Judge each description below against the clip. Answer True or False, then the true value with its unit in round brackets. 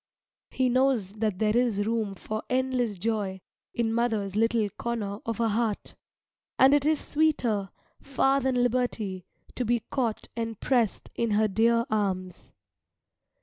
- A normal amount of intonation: True (3.1 semitones)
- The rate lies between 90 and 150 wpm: True (145 wpm)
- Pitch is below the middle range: False (230 Hz)